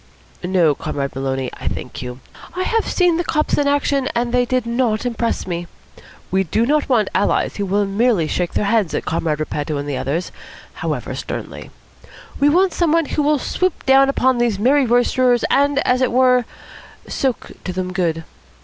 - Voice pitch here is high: Yes, high, 235 Hz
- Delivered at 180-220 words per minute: Yes, average, 185 wpm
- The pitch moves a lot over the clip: Yes, wide, 7.3 semitones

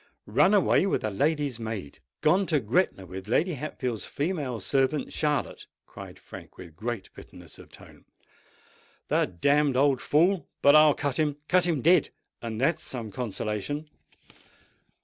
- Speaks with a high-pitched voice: No, medium, 140 Hz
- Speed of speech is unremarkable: No, slow, 130 wpm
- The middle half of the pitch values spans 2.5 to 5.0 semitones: No, wide, 5.4 semitones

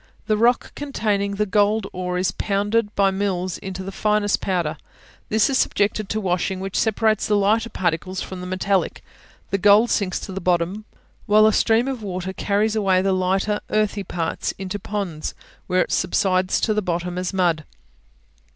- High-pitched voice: Yes, high, 195 Hz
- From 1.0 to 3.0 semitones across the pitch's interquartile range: Yes, narrow, 2.4 semitones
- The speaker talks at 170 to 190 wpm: Yes, average, 175 wpm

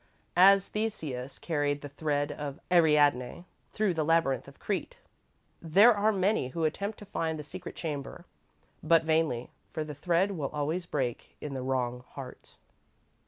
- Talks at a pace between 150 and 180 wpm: Yes, average, 155 wpm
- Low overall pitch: No, medium, 155 Hz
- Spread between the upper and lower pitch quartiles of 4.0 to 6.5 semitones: Yes, average, 4.3 semitones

